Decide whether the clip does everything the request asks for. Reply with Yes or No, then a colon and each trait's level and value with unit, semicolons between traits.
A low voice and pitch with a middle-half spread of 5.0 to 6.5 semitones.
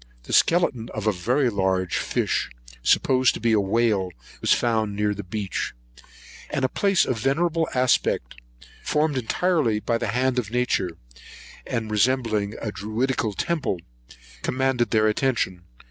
No: low, 115 Hz; average, 4.1 semitones